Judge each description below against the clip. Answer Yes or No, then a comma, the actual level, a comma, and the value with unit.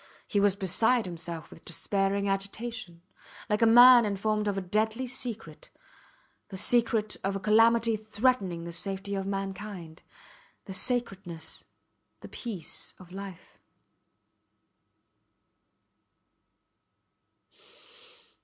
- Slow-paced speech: Yes, slow, 105 wpm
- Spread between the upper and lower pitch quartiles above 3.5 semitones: No, average, 3.1 semitones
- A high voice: Yes, high, 200 Hz